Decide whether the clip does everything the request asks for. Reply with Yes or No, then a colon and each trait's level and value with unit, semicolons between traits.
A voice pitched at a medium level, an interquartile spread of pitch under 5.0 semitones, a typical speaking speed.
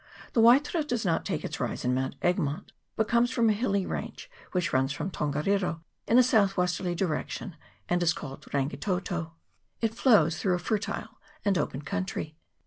No: medium, 180 Hz; wide, 5.5 semitones; average, 180 wpm